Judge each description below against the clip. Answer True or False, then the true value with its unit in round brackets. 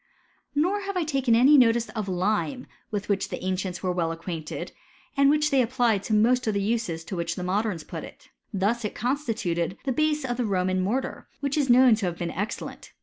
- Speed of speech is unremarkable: False (210 wpm)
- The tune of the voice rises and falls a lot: True (5.9 semitones)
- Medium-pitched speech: False (220 Hz)